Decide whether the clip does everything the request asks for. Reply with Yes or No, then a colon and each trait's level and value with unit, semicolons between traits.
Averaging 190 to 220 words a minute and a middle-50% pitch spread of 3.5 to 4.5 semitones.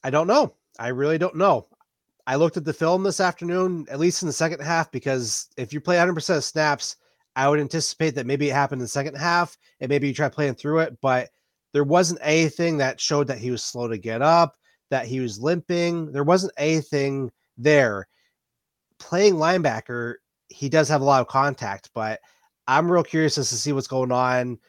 Yes: fast, 205 wpm; average, 4.2 semitones